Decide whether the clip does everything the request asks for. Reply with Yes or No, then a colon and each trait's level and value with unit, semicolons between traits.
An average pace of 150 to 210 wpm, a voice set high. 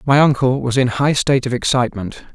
No: fast, 205 wpm; low, 130 Hz